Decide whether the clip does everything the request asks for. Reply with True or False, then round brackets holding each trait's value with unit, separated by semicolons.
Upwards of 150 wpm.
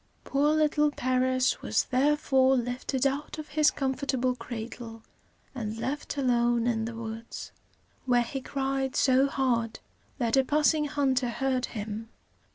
False (135 wpm)